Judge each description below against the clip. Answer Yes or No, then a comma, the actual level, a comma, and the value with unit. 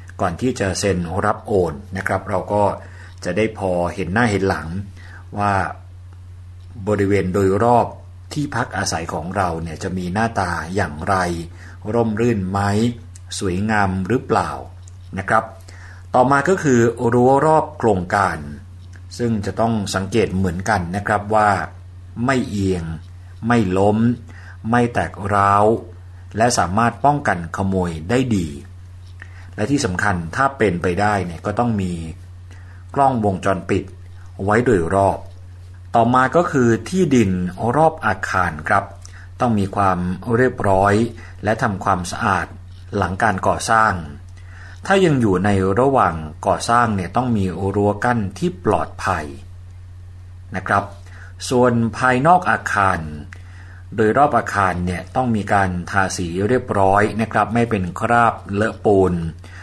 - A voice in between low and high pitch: No, very low, 95 Hz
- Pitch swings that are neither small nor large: Yes, average, 3.4 semitones